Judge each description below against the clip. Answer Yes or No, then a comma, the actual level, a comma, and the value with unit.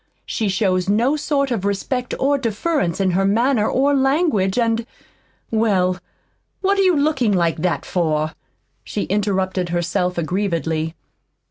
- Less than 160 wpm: Yes, slow, 135 wpm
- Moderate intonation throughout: No, wide, 6.4 semitones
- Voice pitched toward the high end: Yes, high, 200 Hz